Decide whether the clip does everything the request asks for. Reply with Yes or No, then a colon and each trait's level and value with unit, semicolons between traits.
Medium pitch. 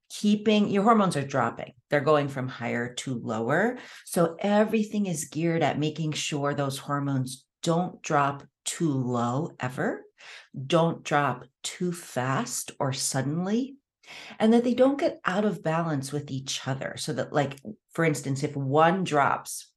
Yes: medium, 155 Hz